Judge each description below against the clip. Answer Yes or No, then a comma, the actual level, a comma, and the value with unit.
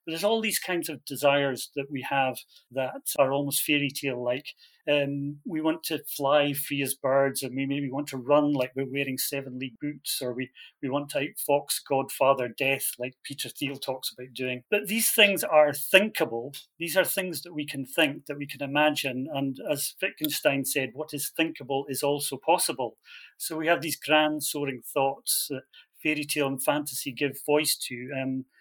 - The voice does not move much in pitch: Yes, narrow, 2.0 semitones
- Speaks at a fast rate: No, average, 190 wpm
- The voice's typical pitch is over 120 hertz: Yes, medium, 140 Hz